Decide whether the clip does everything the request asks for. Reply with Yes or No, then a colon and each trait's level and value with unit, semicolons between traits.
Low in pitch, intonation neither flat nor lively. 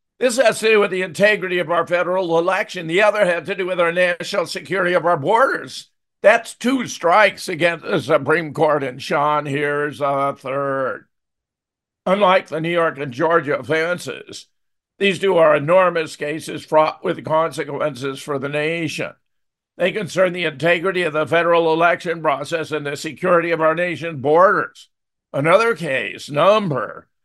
No: medium, 165 Hz; average, 3.1 semitones